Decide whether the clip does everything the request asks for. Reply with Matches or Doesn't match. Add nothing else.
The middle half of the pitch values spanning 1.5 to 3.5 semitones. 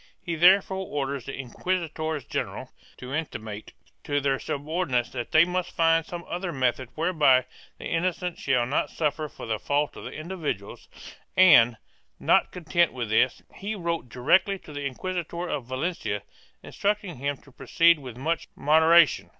Doesn't match